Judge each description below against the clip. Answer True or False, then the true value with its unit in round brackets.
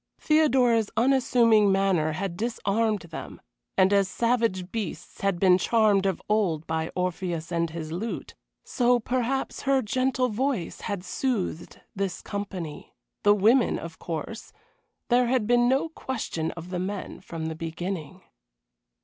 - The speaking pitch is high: True (200 Hz)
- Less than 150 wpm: True (140 wpm)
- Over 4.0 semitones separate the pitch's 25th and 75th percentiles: True (5.3 semitones)